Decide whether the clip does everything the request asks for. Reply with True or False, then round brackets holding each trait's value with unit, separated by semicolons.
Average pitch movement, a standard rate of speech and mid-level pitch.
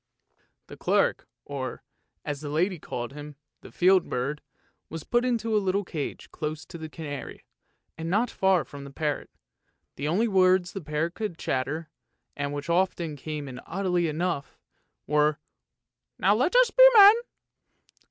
True (4.5 semitones; 160 wpm; 165 Hz)